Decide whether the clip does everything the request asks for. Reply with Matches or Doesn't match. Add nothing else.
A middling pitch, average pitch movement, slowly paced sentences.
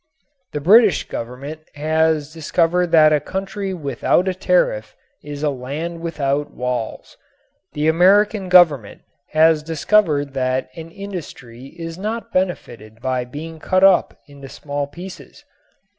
Matches